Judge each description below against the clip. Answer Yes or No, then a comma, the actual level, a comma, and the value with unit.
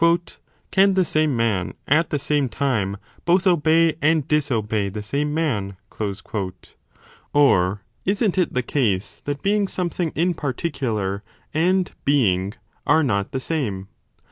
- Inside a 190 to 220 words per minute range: No, average, 140 wpm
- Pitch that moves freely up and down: Yes, wide, 7.7 semitones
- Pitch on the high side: No, medium, 145 Hz